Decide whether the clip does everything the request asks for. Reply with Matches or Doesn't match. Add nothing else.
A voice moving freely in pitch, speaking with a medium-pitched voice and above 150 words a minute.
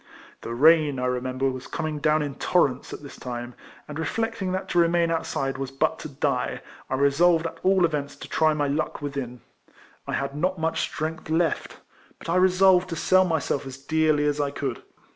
Doesn't match